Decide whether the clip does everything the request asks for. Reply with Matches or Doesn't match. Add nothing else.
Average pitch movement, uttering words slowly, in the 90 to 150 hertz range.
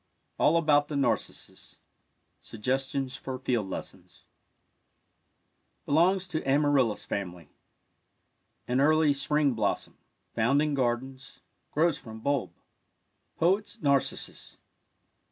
Matches